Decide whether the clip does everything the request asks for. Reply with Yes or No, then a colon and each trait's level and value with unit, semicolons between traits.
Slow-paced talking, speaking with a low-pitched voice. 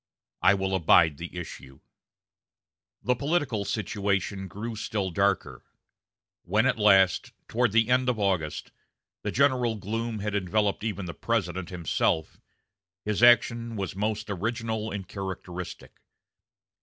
Yes: slow, 125 wpm; low, 105 Hz